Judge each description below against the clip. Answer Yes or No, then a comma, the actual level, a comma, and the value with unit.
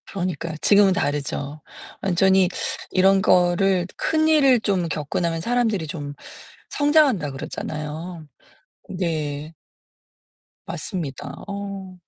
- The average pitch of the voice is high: No, medium, 180 Hz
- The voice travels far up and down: No, average, 4.2 semitones